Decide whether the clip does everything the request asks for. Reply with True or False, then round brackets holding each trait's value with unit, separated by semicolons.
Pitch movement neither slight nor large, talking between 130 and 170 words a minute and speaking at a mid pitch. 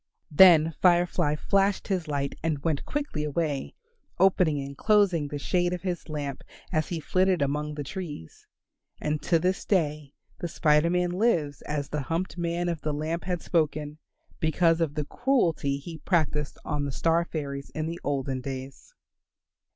True (3.3 semitones; 165 wpm; 160 Hz)